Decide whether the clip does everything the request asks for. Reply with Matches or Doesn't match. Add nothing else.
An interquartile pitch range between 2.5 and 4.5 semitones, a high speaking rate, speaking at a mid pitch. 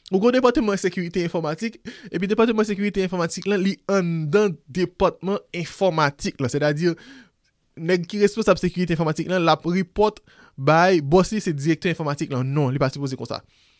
Doesn't match